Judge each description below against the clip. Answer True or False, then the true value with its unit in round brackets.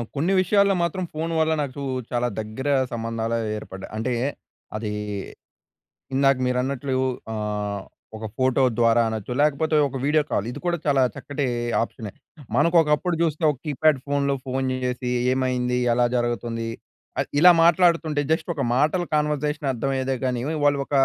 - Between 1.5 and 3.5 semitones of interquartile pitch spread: False (4.0 semitones)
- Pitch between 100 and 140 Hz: True (135 Hz)